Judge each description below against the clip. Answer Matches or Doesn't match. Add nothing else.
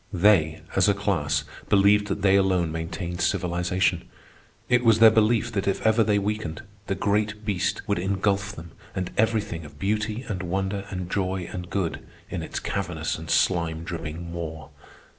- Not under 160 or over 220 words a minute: Matches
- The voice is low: Matches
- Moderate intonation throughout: Matches